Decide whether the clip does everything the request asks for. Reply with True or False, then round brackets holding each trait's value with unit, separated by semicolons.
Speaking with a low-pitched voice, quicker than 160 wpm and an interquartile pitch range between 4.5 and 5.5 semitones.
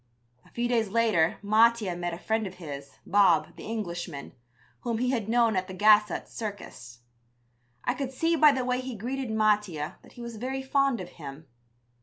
False (215 Hz; 185 wpm; 5.2 semitones)